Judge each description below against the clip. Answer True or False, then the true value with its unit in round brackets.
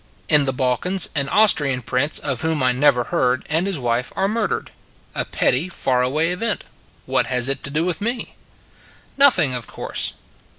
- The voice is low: False (145 Hz)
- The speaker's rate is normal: True (180 wpm)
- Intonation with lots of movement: True (6.0 semitones)